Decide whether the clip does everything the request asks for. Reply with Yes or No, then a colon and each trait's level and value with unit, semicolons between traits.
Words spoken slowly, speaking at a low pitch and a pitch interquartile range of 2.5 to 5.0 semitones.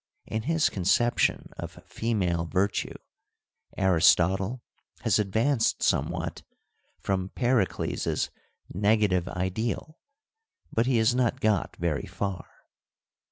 Yes: slow, 95 wpm; low, 105 Hz; average, 4.2 semitones